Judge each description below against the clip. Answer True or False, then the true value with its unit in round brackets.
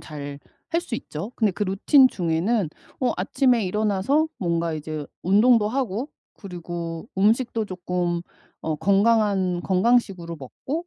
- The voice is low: False (195 Hz)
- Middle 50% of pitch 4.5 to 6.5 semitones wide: True (5.2 semitones)